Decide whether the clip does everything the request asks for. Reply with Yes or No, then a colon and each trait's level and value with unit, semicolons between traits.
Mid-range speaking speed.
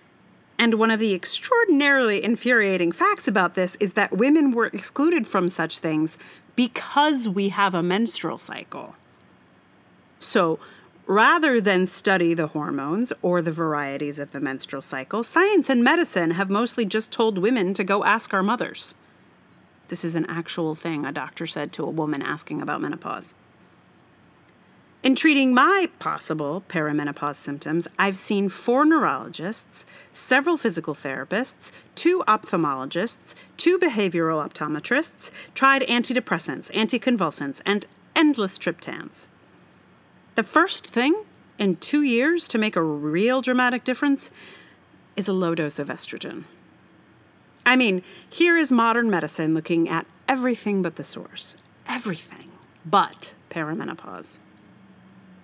No: slow, 130 wpm